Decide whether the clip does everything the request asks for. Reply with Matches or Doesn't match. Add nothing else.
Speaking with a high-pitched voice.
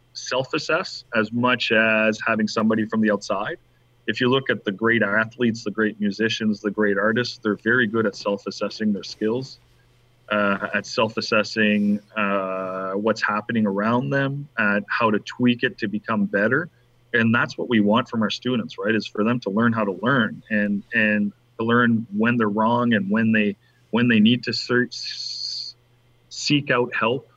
Doesn't match